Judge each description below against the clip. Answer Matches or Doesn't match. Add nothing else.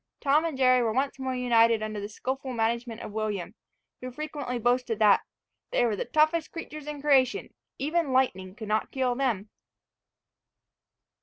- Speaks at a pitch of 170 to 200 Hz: Doesn't match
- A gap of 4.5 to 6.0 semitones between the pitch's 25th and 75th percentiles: Doesn't match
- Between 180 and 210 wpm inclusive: Doesn't match